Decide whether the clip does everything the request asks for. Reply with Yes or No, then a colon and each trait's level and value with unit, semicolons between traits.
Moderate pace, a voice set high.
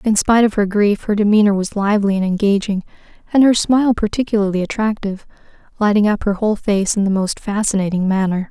Yes: average, 185 wpm; high, 205 Hz